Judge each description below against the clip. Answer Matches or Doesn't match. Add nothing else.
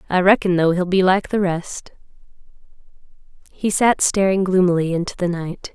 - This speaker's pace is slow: Doesn't match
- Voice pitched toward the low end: Doesn't match